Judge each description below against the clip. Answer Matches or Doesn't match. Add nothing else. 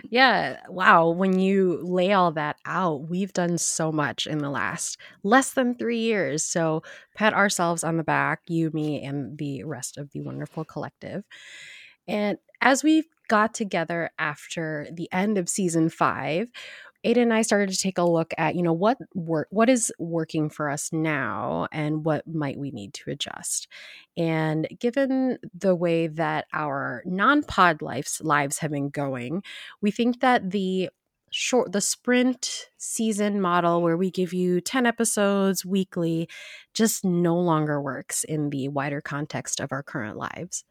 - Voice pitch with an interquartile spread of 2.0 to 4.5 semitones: Doesn't match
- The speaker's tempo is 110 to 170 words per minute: Matches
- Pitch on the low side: Doesn't match